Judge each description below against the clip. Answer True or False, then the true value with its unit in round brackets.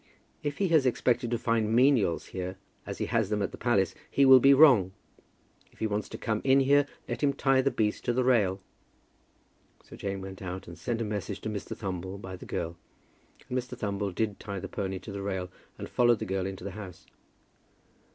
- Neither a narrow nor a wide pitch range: True (4.7 semitones)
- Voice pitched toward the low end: True (105 Hz)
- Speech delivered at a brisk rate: True (215 wpm)